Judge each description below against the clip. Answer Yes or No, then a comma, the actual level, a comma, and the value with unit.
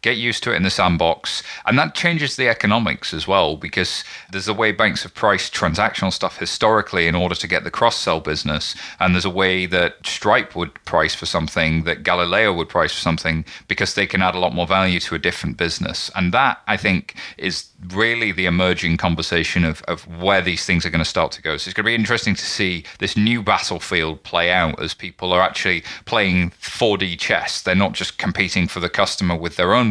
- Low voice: Yes, very low, 90 Hz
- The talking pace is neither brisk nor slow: No, fast, 220 wpm